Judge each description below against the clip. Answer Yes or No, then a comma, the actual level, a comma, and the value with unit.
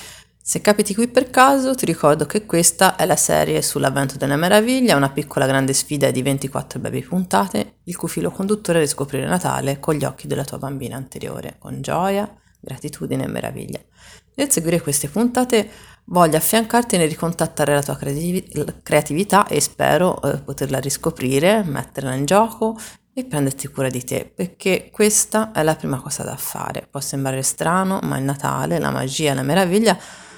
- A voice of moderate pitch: Yes, medium, 160 Hz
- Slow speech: No, average, 165 wpm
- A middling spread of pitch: No, wide, 6.6 semitones